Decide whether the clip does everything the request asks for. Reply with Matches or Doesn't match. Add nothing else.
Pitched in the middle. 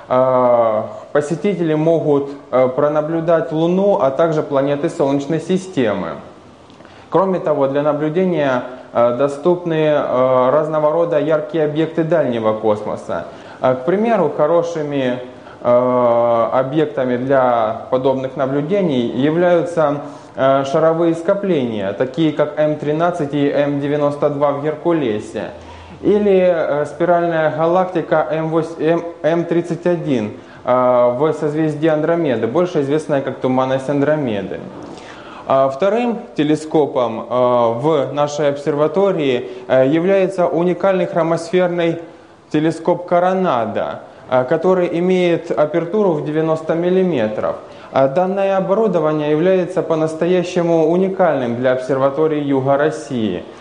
Matches